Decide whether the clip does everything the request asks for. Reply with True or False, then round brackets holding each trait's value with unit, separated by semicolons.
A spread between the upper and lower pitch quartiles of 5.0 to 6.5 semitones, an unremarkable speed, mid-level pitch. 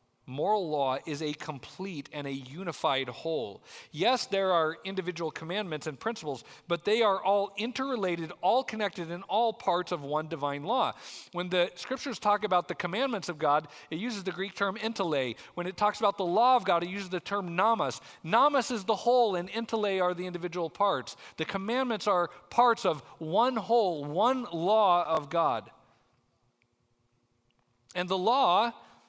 True (5.5 semitones; 170 wpm; 180 Hz)